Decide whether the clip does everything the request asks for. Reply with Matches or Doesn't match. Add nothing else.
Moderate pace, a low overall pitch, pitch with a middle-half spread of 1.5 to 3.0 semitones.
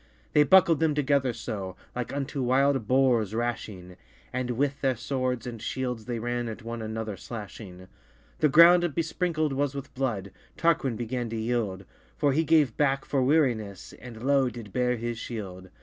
Doesn't match